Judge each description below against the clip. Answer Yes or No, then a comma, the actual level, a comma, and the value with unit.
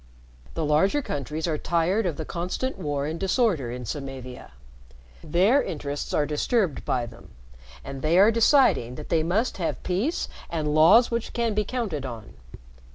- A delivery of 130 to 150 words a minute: No, average, 160 wpm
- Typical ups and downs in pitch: No, wide, 6.7 semitones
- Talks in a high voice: No, medium, 165 Hz